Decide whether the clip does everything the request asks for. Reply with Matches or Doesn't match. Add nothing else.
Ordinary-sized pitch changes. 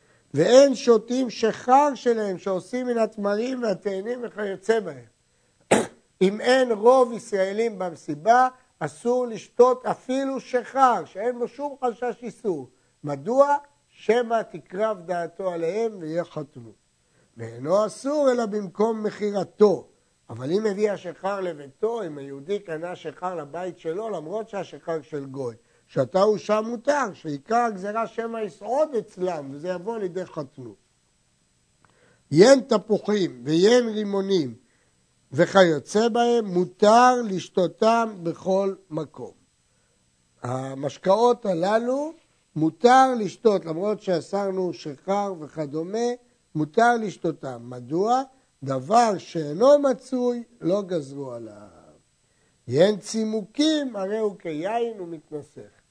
Doesn't match